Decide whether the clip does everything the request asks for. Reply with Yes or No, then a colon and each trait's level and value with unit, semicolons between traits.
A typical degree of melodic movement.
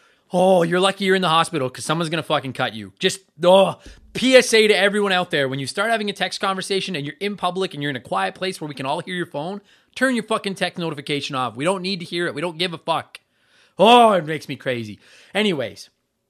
Yes: average, 4.4 semitones